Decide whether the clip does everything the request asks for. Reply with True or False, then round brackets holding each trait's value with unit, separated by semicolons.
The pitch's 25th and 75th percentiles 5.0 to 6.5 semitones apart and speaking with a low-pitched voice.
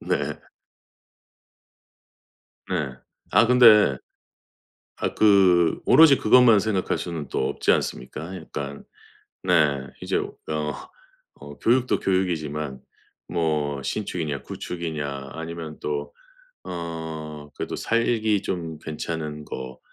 False (4.5 semitones; 80 Hz)